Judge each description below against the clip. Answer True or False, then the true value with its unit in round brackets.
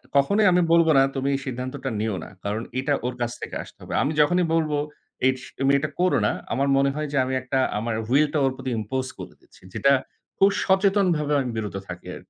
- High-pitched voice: False (135 Hz)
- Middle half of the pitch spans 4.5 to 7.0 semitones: False (3.5 semitones)